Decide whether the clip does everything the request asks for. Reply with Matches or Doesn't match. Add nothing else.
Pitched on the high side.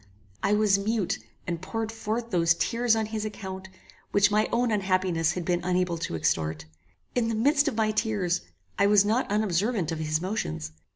Matches